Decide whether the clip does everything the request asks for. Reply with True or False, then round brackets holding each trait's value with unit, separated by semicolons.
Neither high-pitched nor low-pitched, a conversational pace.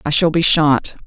False (155 Hz; 225 wpm)